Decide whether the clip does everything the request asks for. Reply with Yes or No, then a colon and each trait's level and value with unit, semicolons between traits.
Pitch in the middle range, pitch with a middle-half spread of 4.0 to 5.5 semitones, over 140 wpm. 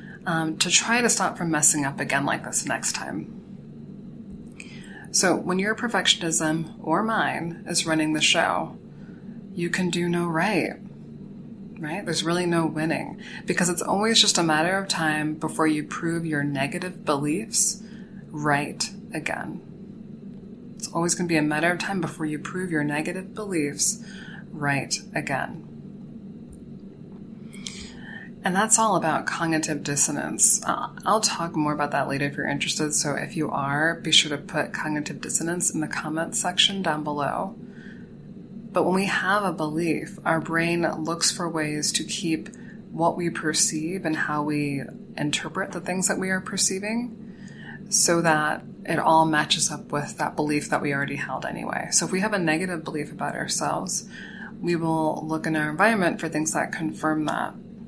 Yes: medium, 170 Hz; average, 4.5 semitones; average, 165 wpm